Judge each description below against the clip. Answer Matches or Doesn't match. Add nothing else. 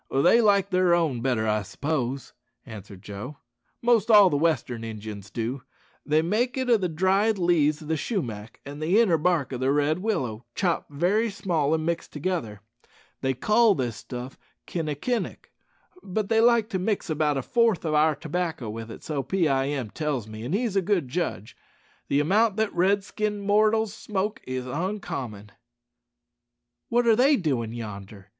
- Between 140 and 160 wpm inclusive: Doesn't match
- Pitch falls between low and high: Matches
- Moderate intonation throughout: Doesn't match